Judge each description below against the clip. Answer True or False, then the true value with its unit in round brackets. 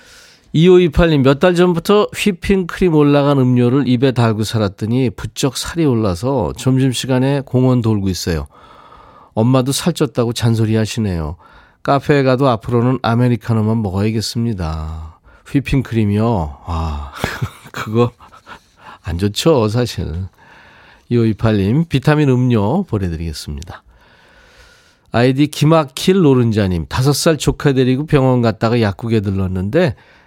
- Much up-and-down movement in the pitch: False (5.0 semitones)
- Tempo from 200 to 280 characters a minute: True (270 characters per minute)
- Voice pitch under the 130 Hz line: True (120 Hz)